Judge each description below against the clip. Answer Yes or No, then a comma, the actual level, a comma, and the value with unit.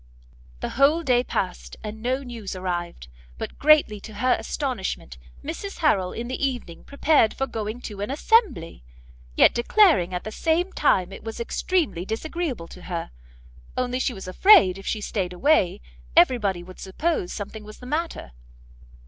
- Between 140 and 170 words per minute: Yes, average, 165 wpm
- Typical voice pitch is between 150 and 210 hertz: No, high, 225 Hz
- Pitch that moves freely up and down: Yes, wide, 7.3 semitones